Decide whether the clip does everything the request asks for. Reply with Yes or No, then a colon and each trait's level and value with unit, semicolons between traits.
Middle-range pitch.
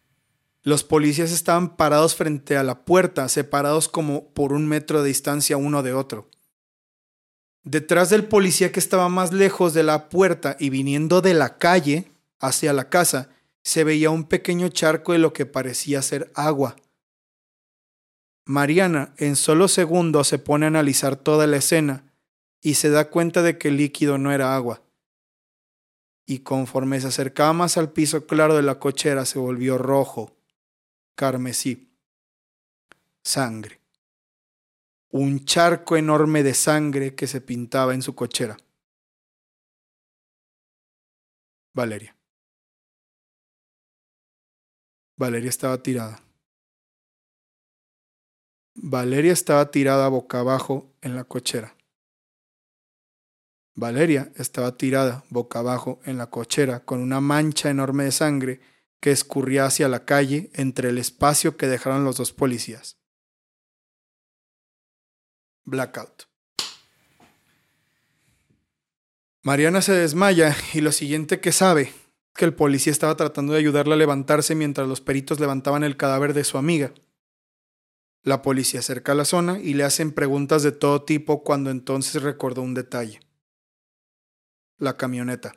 Yes: medium, 145 Hz